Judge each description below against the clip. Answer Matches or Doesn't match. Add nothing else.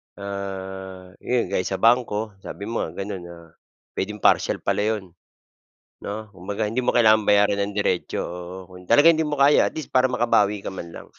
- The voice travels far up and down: Doesn't match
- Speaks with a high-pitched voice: Doesn't match